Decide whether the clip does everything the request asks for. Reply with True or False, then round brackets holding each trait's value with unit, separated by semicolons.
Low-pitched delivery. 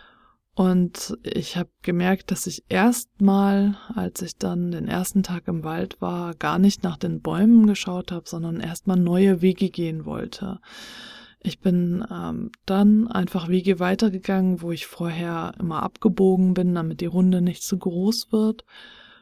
False (185 Hz)